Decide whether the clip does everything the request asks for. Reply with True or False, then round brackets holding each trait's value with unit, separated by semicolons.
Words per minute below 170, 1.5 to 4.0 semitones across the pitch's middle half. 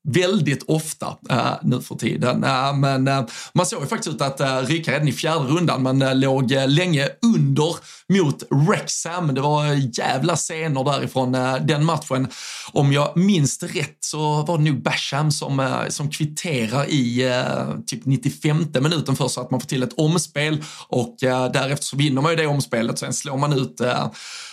False (190 wpm; 3.2 semitones)